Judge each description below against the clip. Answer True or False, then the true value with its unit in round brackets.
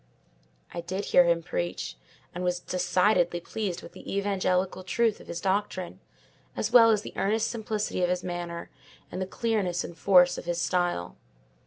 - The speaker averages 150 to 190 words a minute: True (170 wpm)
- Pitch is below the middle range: False (180 Hz)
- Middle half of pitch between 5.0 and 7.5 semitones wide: False (2.5 semitones)